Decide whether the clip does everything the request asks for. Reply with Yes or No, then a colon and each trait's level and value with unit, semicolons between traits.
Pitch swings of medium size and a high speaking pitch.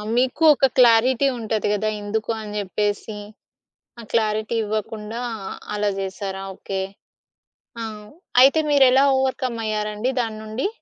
Yes: average, 3.0 semitones; high, 220 Hz